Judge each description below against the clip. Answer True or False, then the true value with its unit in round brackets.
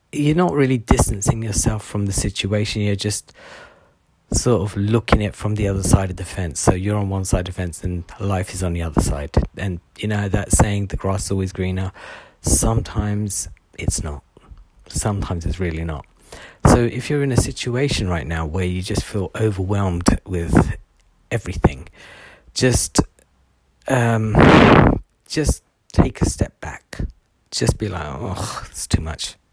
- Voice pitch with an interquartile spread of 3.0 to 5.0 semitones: True (3.3 semitones)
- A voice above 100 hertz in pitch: False (95 Hz)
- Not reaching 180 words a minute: True (170 wpm)